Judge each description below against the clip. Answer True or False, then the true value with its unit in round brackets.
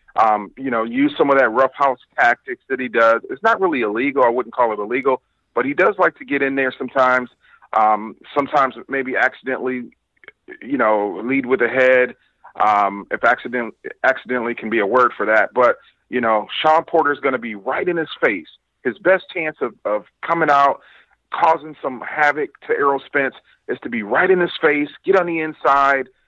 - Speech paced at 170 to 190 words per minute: False (200 wpm)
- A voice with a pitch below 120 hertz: False (135 Hz)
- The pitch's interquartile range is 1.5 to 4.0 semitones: False (4.4 semitones)